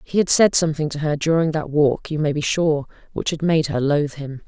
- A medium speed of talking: No, fast, 255 wpm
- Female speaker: Yes, female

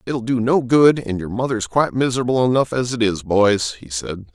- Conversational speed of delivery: No, fast, 220 wpm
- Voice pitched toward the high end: No, low, 115 Hz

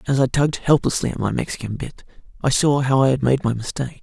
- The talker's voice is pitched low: Yes, low, 130 Hz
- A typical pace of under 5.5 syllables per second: No, 6.6 syllables/s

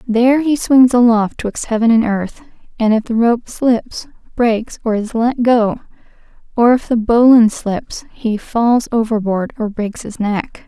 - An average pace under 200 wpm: Yes, average, 170 wpm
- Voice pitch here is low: No, high, 230 Hz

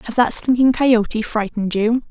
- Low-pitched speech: No, high, 230 Hz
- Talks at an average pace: Yes, average, 170 wpm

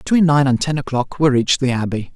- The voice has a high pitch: No, low, 135 Hz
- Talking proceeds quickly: Yes, fast, 250 wpm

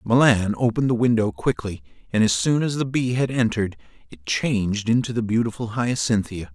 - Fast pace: No, average, 175 wpm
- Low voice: Yes, low, 115 Hz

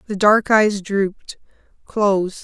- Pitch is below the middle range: No, high, 200 Hz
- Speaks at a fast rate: No, slow, 100 wpm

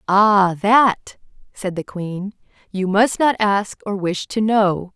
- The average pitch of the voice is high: Yes, high, 200 Hz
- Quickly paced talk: No, average, 155 wpm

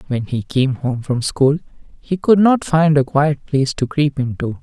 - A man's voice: Yes, male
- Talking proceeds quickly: Yes, fast, 210 wpm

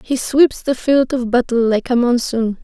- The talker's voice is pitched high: Yes, high, 245 Hz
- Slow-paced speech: No, fast, 205 wpm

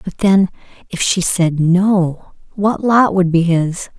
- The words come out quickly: No, average, 165 wpm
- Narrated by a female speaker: Yes, female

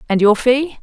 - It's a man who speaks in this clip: No, female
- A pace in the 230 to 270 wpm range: No, fast, 215 wpm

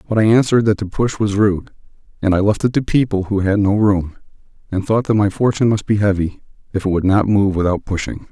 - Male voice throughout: Yes, male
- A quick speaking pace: Yes, fast, 240 wpm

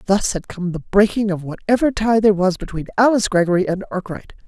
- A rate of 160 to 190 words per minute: No, average, 200 wpm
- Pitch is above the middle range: Yes, high, 200 Hz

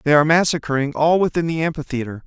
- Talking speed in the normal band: Yes, average, 185 wpm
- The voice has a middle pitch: Yes, medium, 155 Hz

